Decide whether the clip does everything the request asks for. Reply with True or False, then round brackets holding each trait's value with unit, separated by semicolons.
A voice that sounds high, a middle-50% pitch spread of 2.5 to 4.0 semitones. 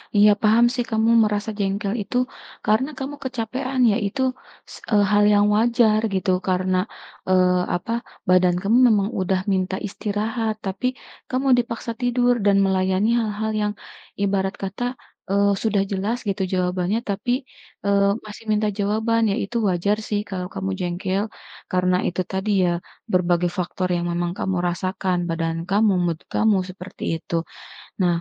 True (200 Hz; 2.9 semitones)